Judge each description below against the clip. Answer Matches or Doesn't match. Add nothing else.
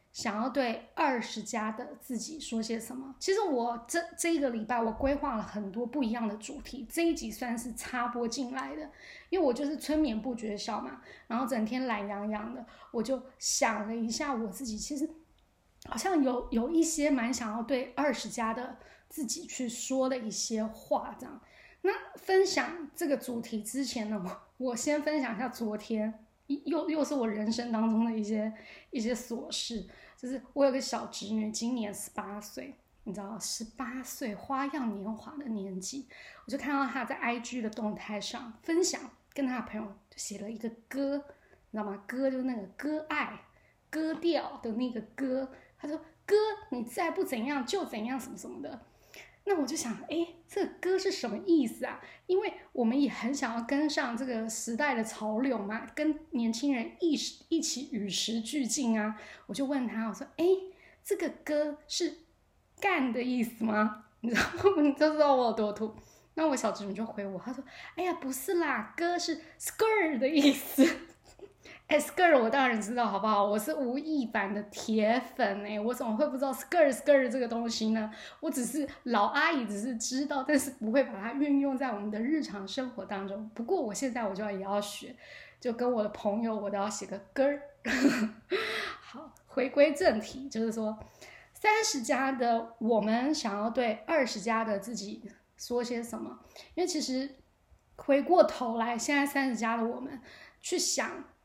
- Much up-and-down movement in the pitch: Doesn't match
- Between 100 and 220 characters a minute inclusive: Doesn't match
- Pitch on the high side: Matches